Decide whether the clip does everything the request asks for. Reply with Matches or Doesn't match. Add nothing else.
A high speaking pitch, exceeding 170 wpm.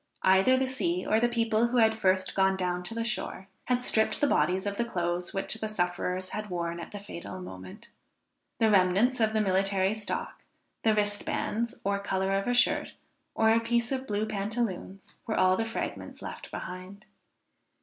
Matches